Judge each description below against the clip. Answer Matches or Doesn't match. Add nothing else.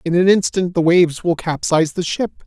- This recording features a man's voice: Matches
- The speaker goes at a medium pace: Doesn't match